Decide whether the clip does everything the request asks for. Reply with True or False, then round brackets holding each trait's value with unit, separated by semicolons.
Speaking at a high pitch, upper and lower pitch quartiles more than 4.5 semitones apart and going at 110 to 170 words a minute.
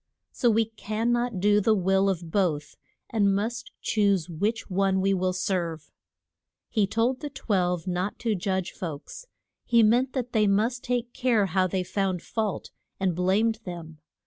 False (200 Hz; 3.7 semitones; 165 wpm)